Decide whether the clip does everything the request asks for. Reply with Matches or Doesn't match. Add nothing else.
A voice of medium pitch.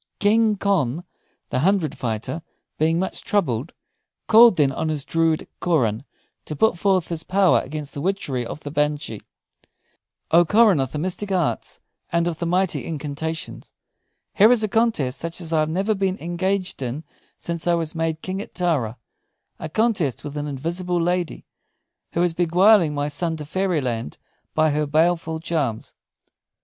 Matches